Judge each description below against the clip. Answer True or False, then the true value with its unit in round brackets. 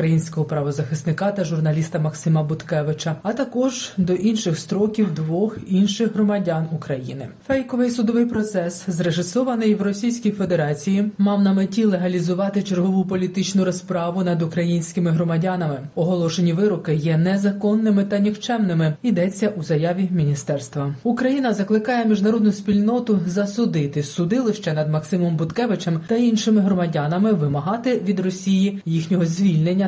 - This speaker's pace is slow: False (120 wpm)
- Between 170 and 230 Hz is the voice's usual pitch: True (185 Hz)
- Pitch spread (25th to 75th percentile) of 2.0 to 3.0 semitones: False (4.2 semitones)